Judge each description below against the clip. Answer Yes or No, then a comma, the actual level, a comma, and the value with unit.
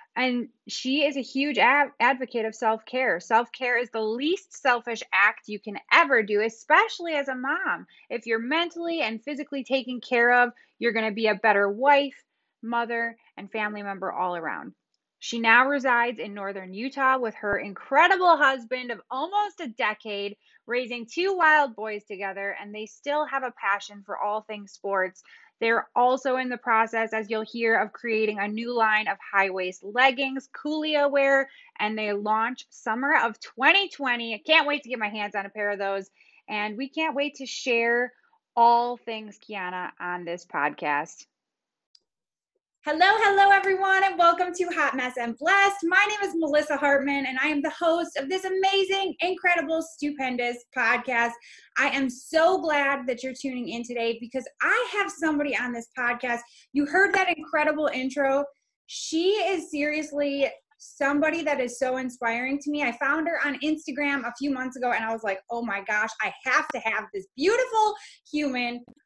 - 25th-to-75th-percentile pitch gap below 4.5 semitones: No, average, 5.2 semitones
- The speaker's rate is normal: Yes, average, 175 wpm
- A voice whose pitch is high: Yes, very high, 255 Hz